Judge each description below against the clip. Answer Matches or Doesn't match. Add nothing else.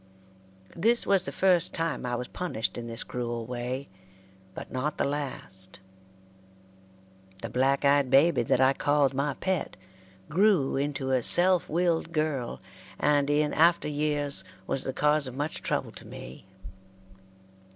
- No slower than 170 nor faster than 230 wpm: Doesn't match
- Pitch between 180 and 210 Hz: Doesn't match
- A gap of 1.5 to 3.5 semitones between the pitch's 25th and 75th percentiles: Doesn't match